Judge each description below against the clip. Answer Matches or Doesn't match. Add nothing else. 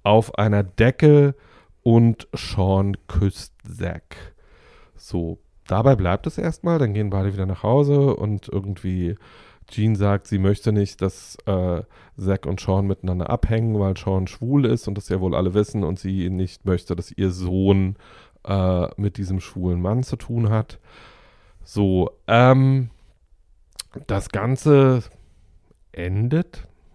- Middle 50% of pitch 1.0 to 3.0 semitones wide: Doesn't match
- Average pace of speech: Matches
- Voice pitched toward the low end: Matches